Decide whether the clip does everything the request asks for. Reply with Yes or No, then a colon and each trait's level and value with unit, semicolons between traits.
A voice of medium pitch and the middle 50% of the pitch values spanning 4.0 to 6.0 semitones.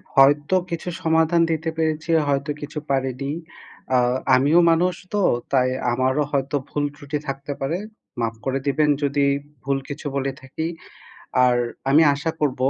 No: medium, 145 Hz; average, 2.8 semitones